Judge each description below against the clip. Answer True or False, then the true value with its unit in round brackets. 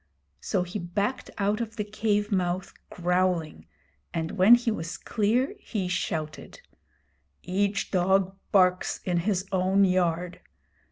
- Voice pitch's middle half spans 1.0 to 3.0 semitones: True (2.5 semitones)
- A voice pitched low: False (190 Hz)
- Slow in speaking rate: True (125 wpm)